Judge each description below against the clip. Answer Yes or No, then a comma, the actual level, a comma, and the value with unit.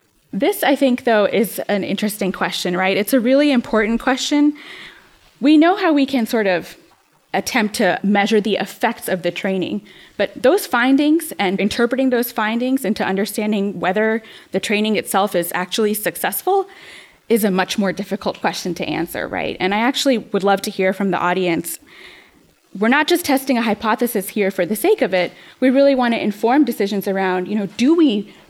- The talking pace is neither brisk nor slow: Yes, average, 185 wpm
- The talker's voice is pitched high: Yes, high, 215 Hz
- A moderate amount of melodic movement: Yes, average, 4.9 semitones